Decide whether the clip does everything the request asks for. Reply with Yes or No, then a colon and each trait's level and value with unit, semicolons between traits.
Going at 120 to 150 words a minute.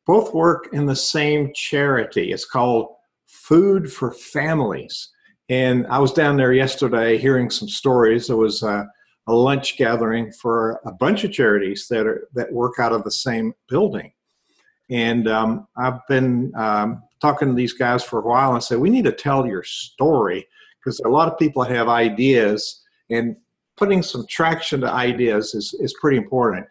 No: average, 175 wpm